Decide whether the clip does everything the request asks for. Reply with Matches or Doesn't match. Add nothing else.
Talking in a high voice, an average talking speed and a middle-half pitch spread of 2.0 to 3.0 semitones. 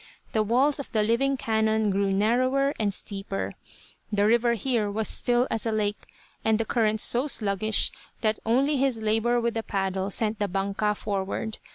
Matches